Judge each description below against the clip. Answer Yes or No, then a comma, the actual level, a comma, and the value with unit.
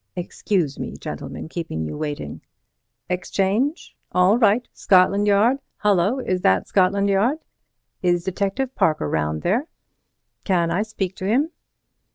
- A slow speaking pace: Yes, slow, 105 wpm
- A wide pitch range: No, average, 3.8 semitones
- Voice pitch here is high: Yes, high, 195 Hz